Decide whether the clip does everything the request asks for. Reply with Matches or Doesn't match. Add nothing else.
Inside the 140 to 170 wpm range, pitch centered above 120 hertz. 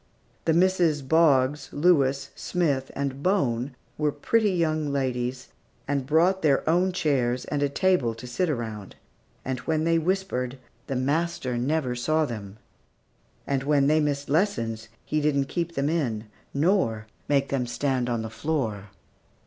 Matches